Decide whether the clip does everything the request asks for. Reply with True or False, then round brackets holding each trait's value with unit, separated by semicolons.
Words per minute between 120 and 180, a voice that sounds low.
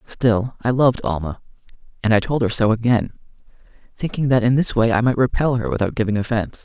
False (200 wpm; 115 Hz)